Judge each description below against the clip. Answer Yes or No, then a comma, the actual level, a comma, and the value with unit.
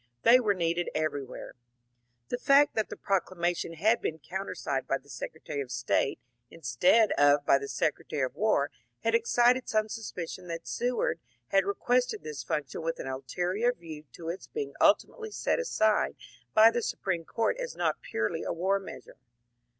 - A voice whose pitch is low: No, medium, 185 Hz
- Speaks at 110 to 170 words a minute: Yes, average, 165 wpm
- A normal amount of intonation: No, wide, 6.7 semitones